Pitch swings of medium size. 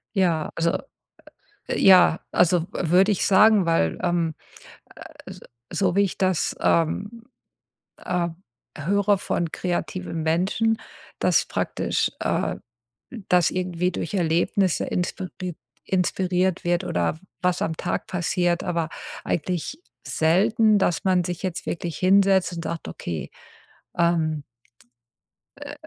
No: narrow, 2.2 semitones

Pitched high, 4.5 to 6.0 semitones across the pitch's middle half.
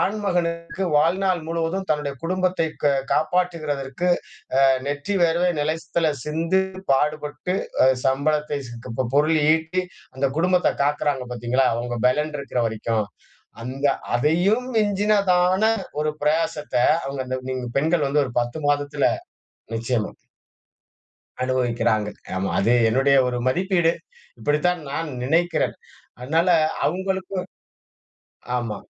No: medium, 150 Hz; average, 5.0 semitones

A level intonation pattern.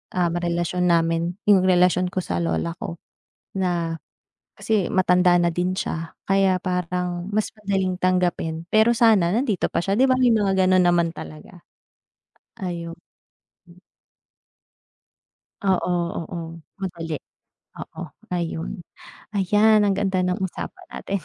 Yes: narrow, 2.1 semitones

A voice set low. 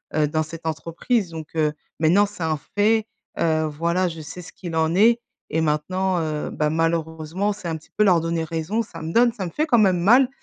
No: medium, 170 Hz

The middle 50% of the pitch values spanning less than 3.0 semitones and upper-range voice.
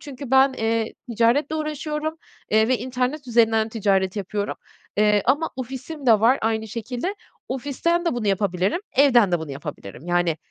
No: average, 4.6 semitones; high, 235 Hz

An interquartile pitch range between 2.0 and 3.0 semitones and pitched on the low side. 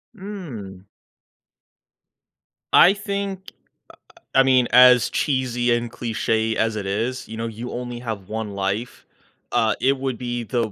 Yes: average, 2.7 semitones; low, 120 Hz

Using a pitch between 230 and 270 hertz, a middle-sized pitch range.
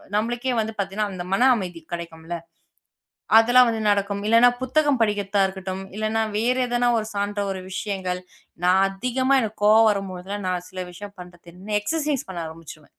No: high, 205 Hz; average, 3.7 semitones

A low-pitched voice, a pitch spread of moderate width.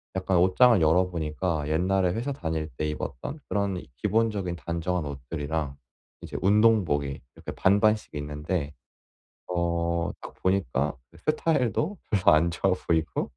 Yes: very low, 90 Hz; average, 4.4 semitones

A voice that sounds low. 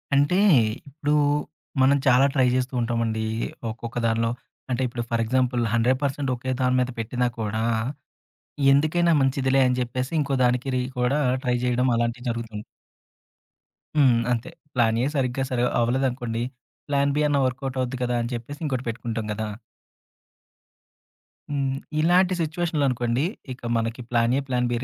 Yes: low, 125 Hz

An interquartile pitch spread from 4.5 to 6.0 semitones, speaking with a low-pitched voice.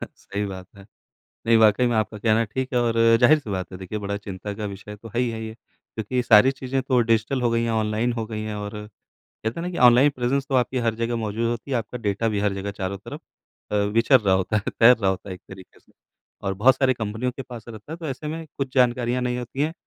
No: average, 3.3 semitones; low, 115 Hz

